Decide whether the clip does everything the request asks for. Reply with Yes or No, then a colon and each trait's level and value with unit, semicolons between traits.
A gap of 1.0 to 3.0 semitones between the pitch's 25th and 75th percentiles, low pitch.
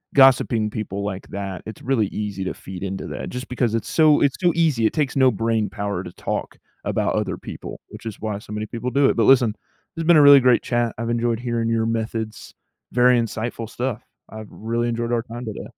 Yes: average, 2.7 semitones; low, 115 Hz